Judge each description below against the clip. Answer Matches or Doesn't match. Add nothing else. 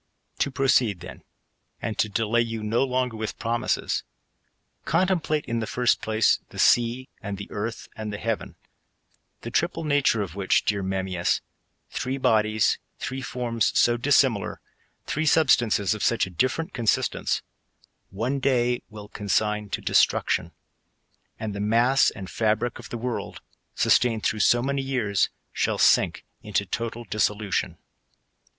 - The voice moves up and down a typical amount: Matches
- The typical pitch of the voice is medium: Doesn't match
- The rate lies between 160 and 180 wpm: Doesn't match